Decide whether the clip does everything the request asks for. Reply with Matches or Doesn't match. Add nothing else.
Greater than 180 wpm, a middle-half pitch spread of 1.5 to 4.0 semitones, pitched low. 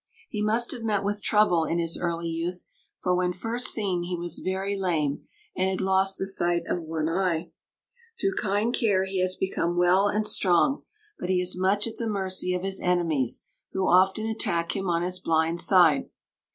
Doesn't match